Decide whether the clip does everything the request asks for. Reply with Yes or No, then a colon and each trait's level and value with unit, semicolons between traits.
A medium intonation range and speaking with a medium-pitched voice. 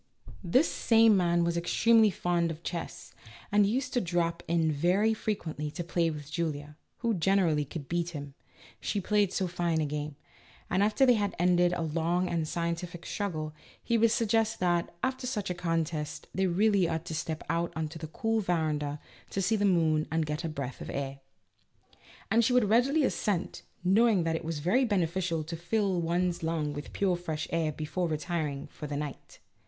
Yes: average, 4.2 semitones; medium, 170 Hz